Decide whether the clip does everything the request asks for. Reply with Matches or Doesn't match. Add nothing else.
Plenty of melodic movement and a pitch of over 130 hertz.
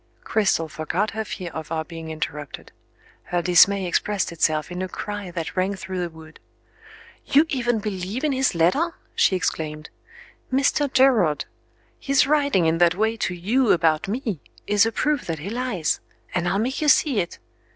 Matches